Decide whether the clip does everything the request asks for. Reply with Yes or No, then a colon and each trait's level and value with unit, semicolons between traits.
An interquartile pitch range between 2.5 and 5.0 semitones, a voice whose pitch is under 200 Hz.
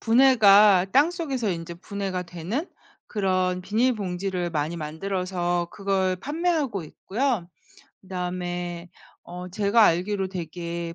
Yes: average, 3.3 semitones; medium, 185 Hz